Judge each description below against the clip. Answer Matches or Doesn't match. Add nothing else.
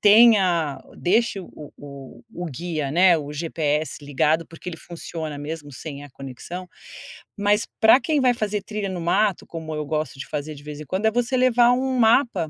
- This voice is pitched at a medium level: Matches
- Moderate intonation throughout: Doesn't match